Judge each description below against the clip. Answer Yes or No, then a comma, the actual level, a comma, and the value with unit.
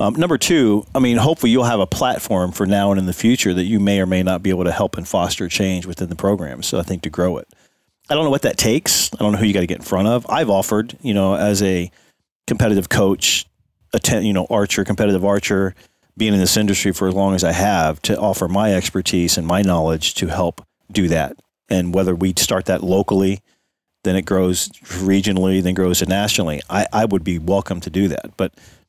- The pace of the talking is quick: Yes, fast, 235 wpm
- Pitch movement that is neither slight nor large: No, narrow, 1.8 semitones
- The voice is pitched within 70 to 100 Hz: Yes, very low, 95 Hz